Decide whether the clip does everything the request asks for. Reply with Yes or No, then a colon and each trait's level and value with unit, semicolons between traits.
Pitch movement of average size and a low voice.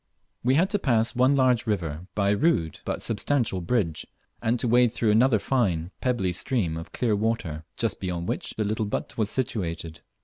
No: wide, 5.8 semitones; low, 110 Hz